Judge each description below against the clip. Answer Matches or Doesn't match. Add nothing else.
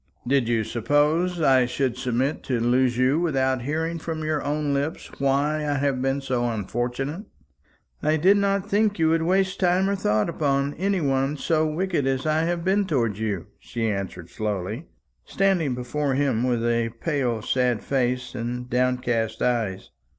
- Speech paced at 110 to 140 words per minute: Doesn't match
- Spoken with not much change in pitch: Doesn't match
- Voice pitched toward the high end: Doesn't match